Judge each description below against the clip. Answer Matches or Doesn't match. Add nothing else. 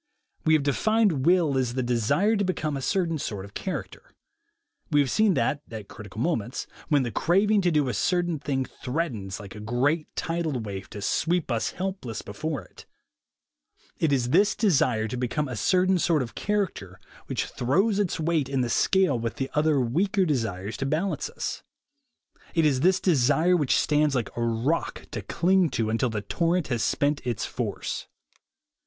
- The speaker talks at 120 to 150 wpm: Doesn't match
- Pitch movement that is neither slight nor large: Doesn't match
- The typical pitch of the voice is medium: Matches